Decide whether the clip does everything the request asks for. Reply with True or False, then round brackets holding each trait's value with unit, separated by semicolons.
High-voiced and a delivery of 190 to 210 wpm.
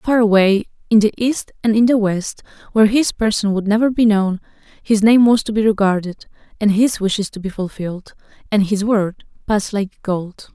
True (210 Hz; 195 wpm)